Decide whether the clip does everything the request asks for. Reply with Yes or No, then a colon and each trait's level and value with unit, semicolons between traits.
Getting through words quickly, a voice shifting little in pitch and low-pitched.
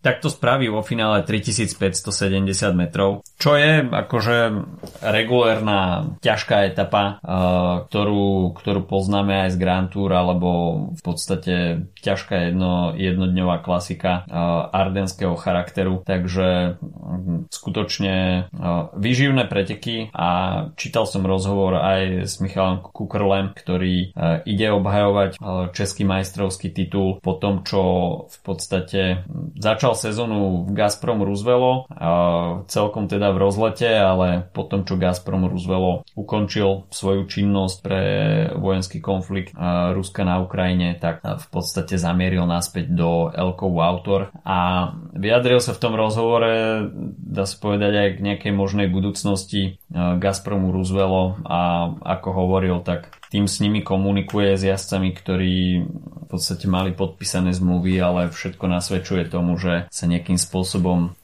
No: average, 125 wpm; narrow, 2.0 semitones; very low, 95 Hz